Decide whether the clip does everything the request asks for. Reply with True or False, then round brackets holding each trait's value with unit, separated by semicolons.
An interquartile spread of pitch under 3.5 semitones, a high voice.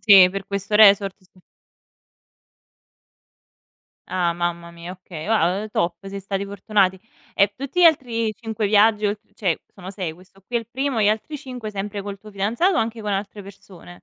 True (2.7 semitones; 200 Hz)